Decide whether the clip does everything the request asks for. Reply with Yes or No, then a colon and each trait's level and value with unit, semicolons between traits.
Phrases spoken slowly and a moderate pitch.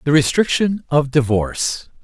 Yes: slow, 120 wpm; medium, 145 Hz